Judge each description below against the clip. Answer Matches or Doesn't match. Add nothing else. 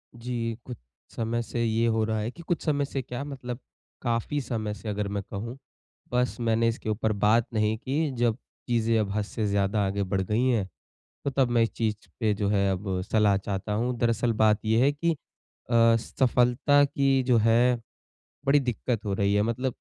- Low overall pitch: Matches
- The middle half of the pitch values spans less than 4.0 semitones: Matches